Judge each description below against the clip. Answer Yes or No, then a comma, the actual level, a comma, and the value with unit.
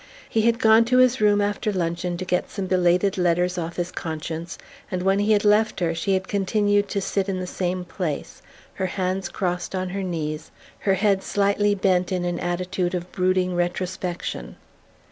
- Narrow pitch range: Yes, narrow, 2.3 semitones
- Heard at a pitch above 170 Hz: Yes, medium, 185 Hz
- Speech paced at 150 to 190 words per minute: Yes, average, 185 wpm